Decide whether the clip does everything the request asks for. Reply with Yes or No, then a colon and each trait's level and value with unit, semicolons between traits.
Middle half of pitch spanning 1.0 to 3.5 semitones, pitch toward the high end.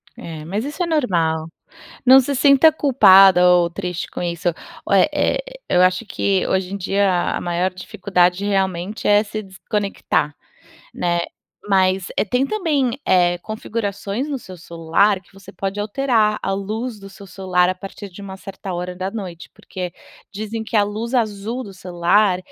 Yes: average, 3.2 semitones; high, 195 Hz